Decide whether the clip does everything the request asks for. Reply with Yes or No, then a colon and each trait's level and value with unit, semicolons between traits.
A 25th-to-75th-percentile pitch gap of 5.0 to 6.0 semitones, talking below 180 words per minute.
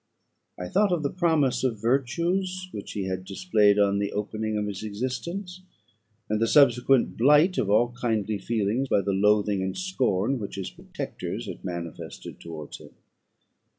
Yes: wide, 5.5 semitones; average, 160 wpm